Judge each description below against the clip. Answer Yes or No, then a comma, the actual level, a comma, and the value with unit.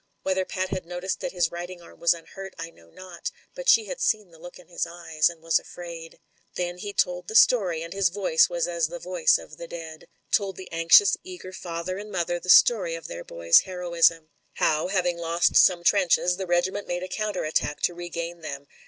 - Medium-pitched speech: Yes, medium, 175 Hz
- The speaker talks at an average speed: No, fast, 215 wpm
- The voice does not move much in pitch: Yes, narrow, 2.0 semitones